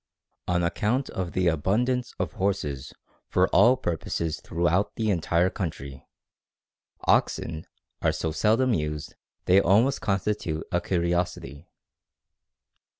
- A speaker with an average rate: No, slow, 115 wpm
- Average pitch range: Yes, average, 4.4 semitones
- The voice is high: No, very low, 90 Hz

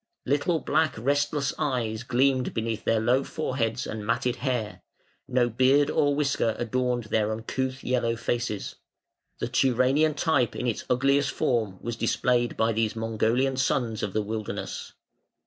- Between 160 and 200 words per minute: No, average, 145 wpm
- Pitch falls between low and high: No, low, 125 Hz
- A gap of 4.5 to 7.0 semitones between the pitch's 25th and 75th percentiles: No, average, 3.2 semitones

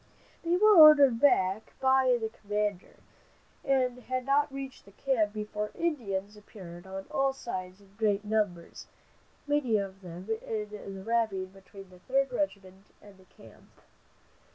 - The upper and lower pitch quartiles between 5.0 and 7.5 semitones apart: Yes, wide, 5.4 semitones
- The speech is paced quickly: No, average, 140 wpm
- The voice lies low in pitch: No, high, 210 Hz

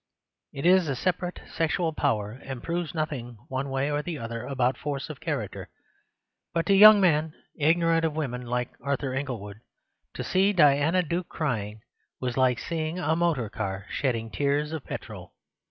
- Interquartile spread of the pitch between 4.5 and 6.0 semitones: Yes, average, 5.0 semitones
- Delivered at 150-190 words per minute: Yes, average, 165 wpm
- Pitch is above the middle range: No, medium, 145 Hz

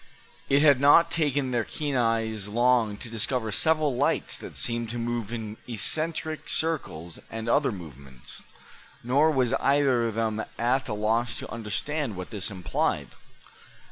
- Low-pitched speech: Yes, low, 120 Hz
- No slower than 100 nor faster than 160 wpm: Yes, average, 150 wpm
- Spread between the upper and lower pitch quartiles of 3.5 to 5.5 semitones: Yes, average, 4.3 semitones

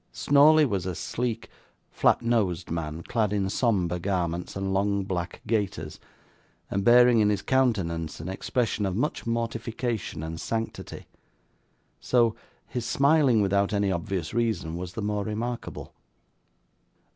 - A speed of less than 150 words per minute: Yes, slow, 135 wpm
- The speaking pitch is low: Yes, low, 105 Hz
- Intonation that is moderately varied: Yes, average, 4.3 semitones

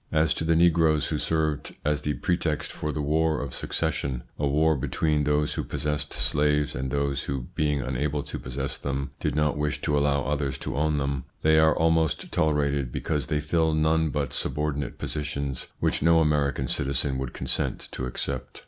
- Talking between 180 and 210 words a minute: Yes, average, 185 wpm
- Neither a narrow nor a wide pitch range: No, narrow, 1.9 semitones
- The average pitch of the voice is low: Yes, very low, 75 Hz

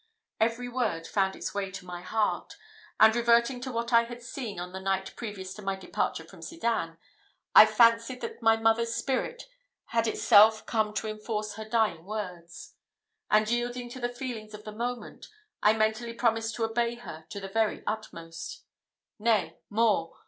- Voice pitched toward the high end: Yes, high, 220 Hz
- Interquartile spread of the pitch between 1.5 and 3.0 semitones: Yes, narrow, 2.4 semitones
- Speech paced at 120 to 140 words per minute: No, average, 170 wpm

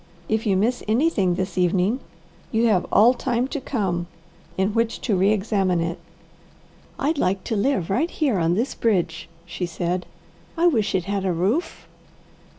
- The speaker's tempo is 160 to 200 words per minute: Yes, average, 165 wpm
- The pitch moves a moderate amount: Yes, average, 4.6 semitones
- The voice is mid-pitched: No, high, 200 Hz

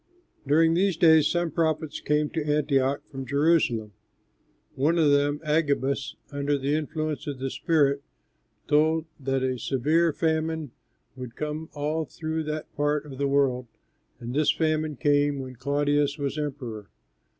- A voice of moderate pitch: Yes, medium, 145 Hz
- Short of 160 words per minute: Yes, average, 145 wpm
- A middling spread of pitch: No, narrow, 2.2 semitones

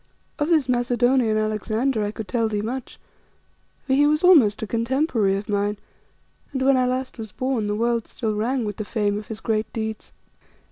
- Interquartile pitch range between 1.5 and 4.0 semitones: Yes, average, 3.5 semitones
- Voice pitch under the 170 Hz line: No, high, 230 Hz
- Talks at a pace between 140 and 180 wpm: No, average, 190 wpm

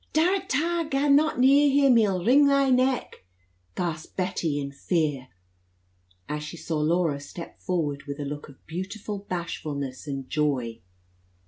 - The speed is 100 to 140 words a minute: No, average, 150 wpm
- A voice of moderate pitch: Yes, medium, 175 Hz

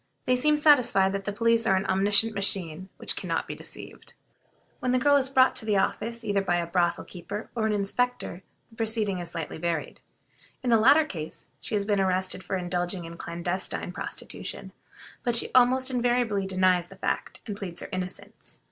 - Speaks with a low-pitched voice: No, high, 200 Hz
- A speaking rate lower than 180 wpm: No, average, 190 wpm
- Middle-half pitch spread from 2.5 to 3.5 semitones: No, average, 4.3 semitones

